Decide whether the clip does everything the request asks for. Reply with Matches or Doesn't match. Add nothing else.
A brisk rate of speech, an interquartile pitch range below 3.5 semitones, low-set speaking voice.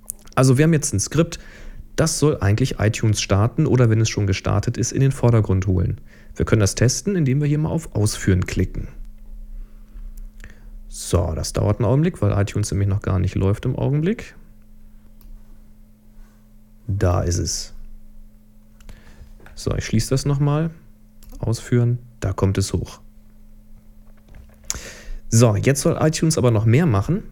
Doesn't match